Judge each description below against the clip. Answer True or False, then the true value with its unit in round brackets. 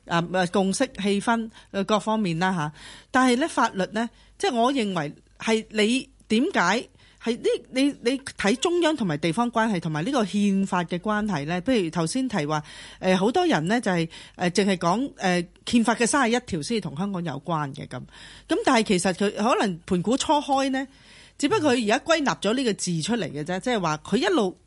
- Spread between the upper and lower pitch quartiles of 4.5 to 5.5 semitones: True (5.1 semitones)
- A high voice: True (210 Hz)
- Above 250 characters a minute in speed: True (275 characters per minute)